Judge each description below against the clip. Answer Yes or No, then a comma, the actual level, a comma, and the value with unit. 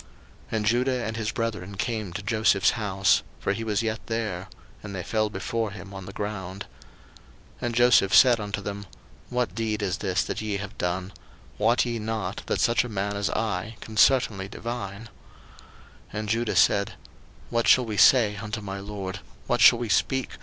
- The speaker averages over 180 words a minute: Yes, average, 190 wpm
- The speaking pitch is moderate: No, low, 105 Hz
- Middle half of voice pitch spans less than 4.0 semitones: Yes, narrow, 2.5 semitones